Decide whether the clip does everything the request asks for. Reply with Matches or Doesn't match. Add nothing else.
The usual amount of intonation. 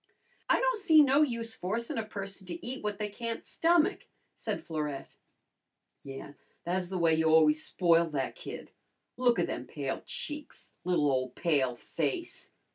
Doesn't match